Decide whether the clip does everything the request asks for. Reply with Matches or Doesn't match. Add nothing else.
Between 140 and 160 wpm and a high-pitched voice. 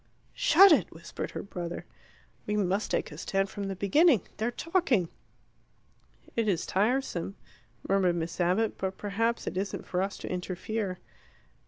Matches